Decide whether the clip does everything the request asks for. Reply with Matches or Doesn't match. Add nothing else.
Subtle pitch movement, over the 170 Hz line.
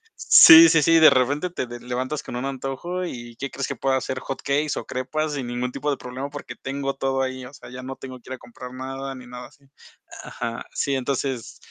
Doesn't match